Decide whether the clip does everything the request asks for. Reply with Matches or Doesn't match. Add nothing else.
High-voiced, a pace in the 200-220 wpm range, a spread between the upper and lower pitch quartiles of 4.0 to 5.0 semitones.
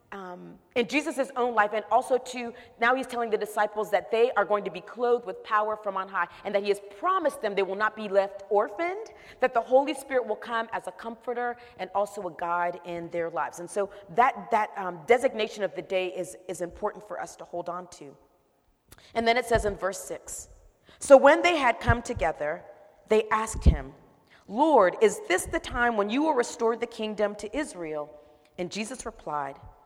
Matches